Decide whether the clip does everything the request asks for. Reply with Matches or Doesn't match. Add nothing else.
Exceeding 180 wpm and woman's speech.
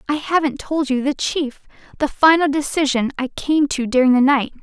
Matches